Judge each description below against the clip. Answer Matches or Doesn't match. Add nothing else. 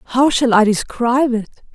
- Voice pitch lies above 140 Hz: Matches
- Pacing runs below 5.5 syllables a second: Matches